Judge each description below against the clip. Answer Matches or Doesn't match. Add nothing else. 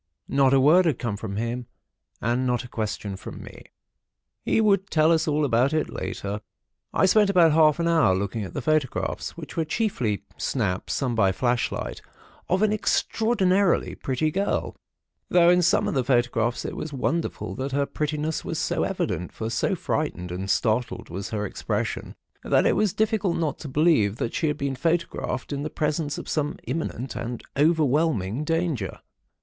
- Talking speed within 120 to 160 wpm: Doesn't match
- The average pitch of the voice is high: Doesn't match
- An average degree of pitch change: Doesn't match